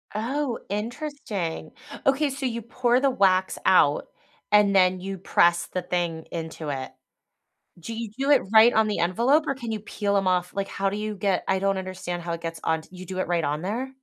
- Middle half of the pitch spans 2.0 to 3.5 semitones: No, average, 4.7 semitones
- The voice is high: Yes, high, 195 Hz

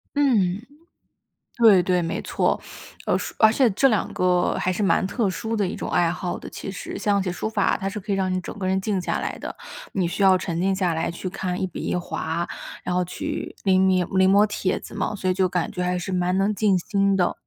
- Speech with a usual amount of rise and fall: No, narrow, 2.0 semitones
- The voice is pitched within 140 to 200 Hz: Yes, high, 190 Hz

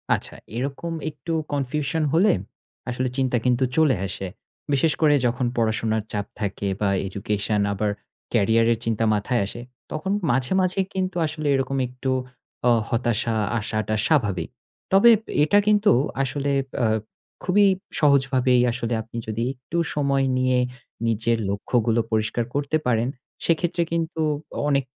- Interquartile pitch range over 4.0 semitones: Yes, average, 4.9 semitones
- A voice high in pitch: No, low, 125 Hz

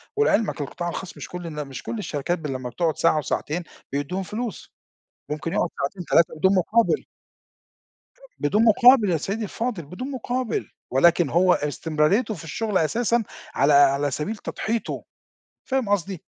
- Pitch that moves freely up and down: Yes, wide, 6.5 semitones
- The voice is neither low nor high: Yes, medium, 180 Hz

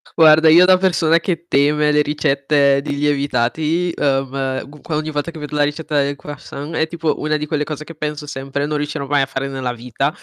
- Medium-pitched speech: Yes, medium, 150 Hz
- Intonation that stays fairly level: Yes, narrow, 2.0 semitones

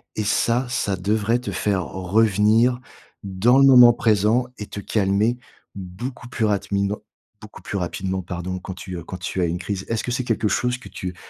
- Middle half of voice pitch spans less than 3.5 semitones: No, average, 3.9 semitones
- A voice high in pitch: No, low, 105 Hz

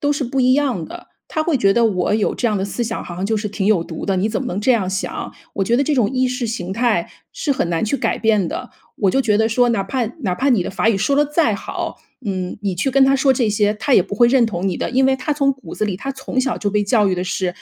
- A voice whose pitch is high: Yes, high, 220 Hz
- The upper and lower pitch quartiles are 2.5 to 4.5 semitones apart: No, average, 5.0 semitones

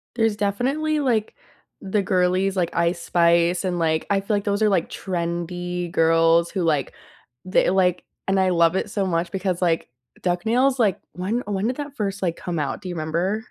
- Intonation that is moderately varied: Yes, average, 3.2 semitones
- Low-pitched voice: No, medium, 185 Hz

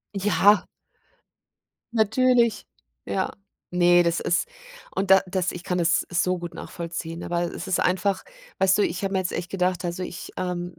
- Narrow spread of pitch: Yes, narrow, 1.9 semitones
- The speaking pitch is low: No, medium, 180 Hz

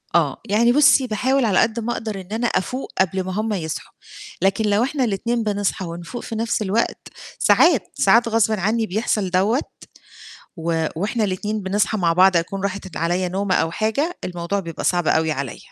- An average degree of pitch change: Yes, average, 3.8 semitones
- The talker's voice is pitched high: Yes, high, 200 Hz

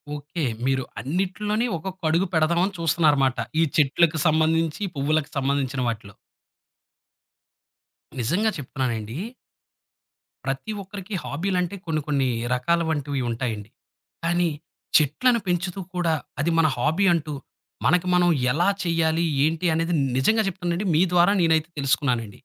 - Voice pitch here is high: No, medium, 160 Hz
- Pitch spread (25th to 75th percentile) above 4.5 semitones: No, average, 4.2 semitones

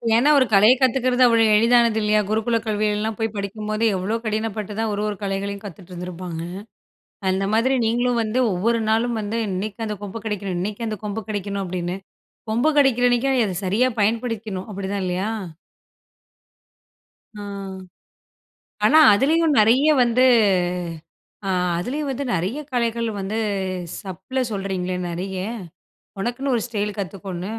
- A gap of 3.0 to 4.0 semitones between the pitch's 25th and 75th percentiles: Yes, average, 3.3 semitones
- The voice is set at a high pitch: Yes, high, 215 Hz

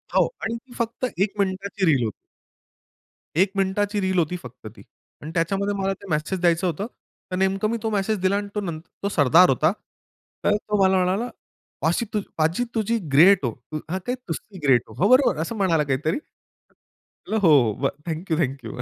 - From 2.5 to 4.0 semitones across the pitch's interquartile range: No, average, 4.5 semitones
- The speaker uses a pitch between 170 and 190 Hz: Yes, medium, 185 Hz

